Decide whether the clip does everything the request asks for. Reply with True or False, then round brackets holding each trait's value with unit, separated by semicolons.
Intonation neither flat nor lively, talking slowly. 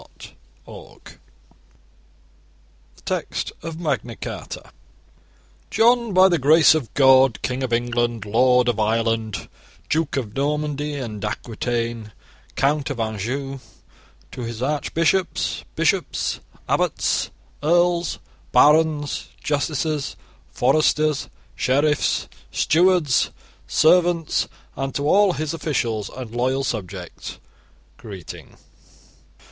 True (4.9 semitones; 95 wpm)